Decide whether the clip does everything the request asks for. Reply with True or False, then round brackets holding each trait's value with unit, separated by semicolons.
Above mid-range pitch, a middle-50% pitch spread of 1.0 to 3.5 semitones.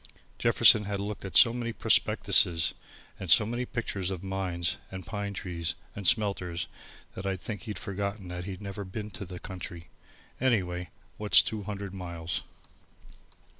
False (95 Hz; 2.8 semitones)